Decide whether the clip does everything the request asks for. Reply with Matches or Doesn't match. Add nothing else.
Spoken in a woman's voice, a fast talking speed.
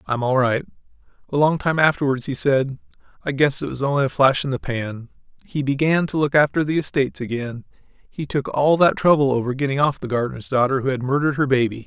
Doesn't match